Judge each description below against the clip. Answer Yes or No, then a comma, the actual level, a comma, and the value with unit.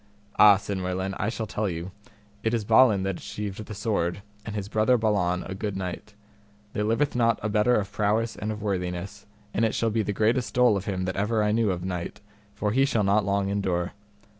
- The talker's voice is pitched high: No, low, 105 Hz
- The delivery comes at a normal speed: No, fast, 215 wpm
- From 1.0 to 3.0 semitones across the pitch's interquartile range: Yes, narrow, 2.4 semitones